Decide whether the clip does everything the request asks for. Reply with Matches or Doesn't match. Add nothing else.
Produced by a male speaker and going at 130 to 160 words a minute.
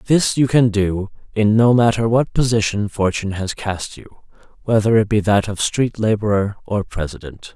Doesn't match